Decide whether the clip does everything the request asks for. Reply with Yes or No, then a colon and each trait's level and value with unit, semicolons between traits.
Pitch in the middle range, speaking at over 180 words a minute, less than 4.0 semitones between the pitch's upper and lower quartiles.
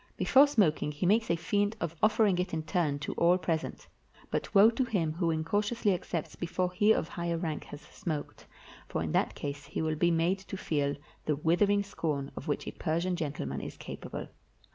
No: medium, 170 Hz; average, 195 wpm; average, 4.3 semitones